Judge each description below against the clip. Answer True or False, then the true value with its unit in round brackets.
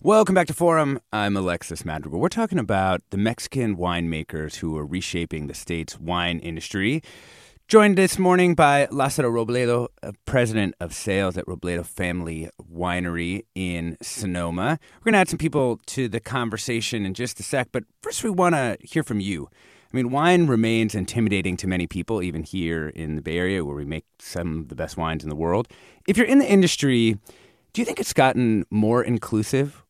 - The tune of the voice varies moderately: False (7.3 semitones)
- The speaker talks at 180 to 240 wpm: True (190 wpm)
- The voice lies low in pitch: True (105 Hz)